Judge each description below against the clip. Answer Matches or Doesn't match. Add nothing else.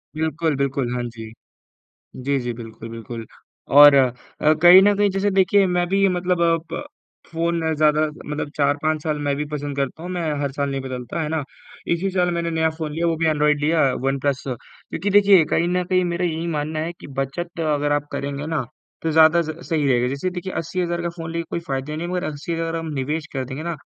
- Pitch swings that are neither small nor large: Matches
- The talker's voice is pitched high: Doesn't match